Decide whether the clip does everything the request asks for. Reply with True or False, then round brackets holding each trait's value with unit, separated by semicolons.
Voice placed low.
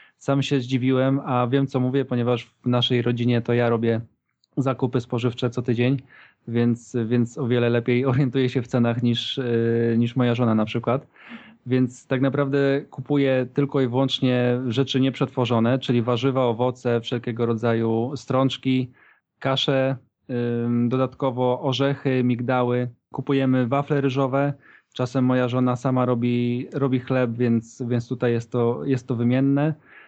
True (125 Hz)